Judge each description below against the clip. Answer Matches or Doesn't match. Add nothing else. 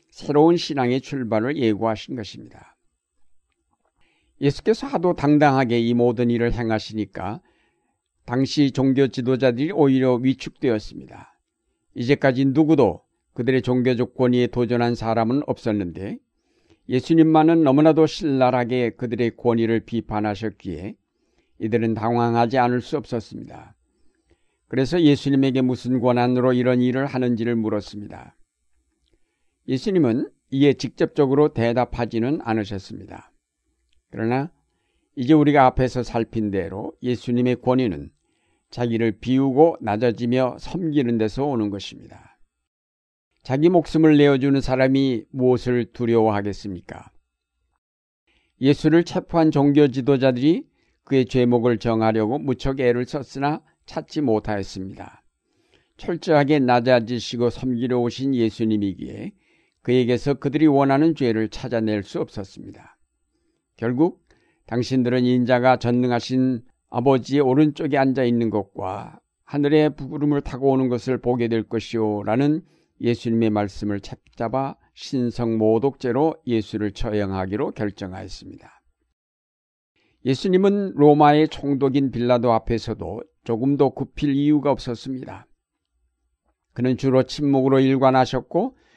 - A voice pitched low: Matches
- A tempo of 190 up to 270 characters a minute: Doesn't match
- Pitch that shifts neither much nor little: Matches